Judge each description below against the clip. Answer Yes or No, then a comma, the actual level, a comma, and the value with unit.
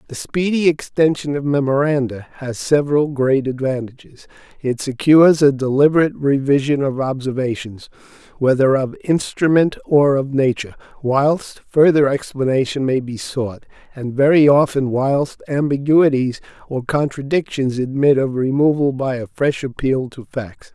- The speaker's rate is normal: No, slow, 125 wpm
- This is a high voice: No, low, 135 Hz